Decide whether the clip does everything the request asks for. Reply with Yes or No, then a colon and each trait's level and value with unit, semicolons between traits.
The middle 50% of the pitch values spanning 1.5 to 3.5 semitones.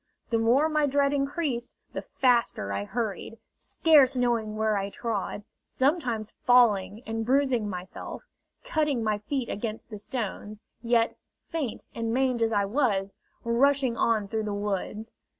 No: average, 3.9 semitones